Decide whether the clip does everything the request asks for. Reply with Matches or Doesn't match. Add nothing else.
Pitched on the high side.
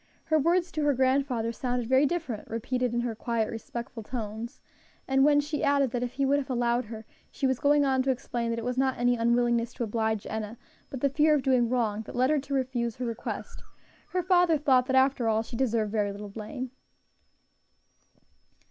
Matches